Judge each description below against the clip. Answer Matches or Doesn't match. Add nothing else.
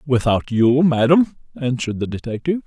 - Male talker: Matches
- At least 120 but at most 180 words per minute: Matches